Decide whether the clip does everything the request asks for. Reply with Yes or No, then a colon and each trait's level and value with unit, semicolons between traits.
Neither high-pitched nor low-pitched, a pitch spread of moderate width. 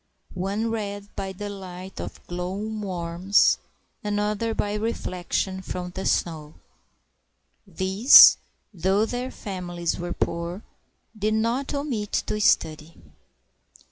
No: high, 195 Hz; average, 3.1 semitones